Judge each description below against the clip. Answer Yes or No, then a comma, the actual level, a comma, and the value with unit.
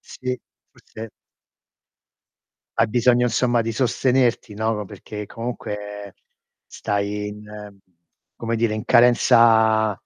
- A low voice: Yes, low, 110 Hz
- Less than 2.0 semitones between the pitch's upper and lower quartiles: No, narrow, 2.4 semitones